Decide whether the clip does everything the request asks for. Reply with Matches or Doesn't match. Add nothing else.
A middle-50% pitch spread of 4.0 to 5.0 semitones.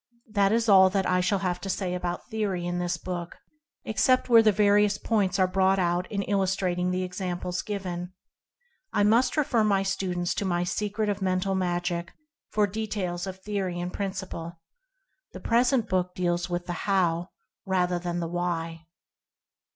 Doesn't match